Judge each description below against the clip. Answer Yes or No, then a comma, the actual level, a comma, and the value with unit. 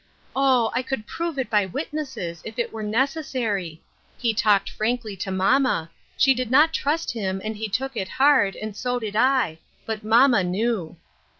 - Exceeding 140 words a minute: Yes, average, 175 wpm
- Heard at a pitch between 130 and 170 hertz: No, high, 225 Hz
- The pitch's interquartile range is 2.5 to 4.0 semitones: No, average, 4.6 semitones